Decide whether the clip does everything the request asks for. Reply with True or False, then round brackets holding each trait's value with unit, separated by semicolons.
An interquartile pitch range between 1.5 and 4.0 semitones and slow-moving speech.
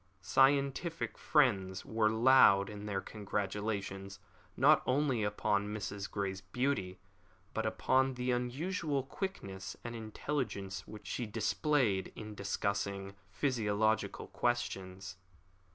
False (4.8 semitones; 105 wpm)